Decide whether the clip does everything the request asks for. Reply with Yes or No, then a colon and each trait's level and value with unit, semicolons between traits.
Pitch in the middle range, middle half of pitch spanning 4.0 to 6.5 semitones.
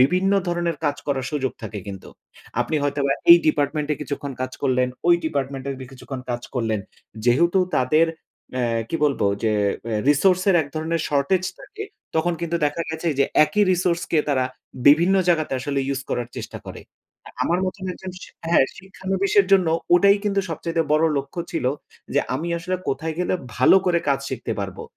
Yes: medium, 155 Hz; average, 4.7 semitones